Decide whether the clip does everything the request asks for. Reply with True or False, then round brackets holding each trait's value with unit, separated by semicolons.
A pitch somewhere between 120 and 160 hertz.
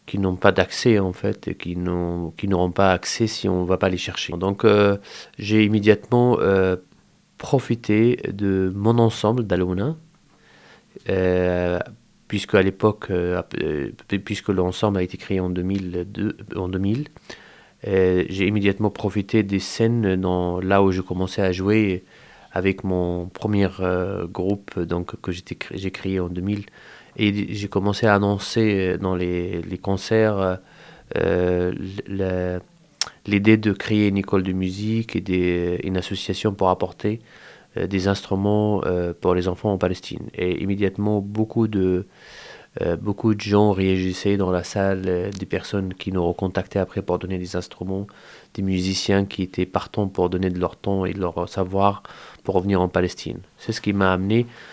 False (95 Hz)